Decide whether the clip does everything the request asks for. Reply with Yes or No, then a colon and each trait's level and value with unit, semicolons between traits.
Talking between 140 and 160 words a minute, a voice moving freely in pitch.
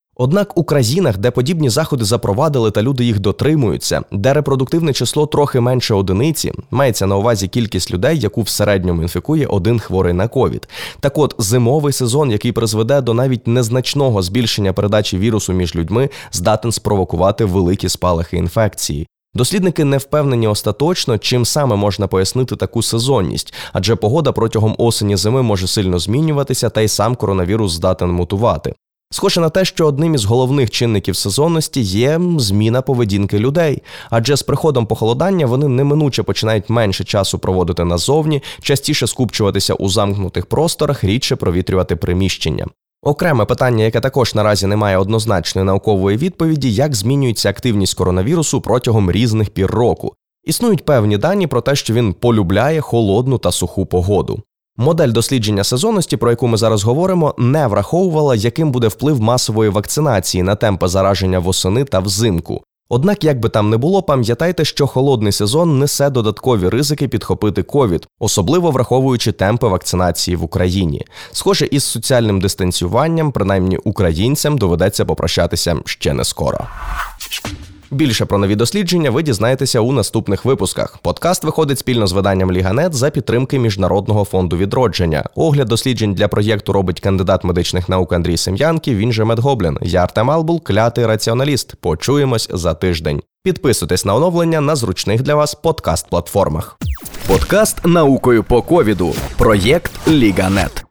Yes: average, 145 wpm; wide, 6.1 semitones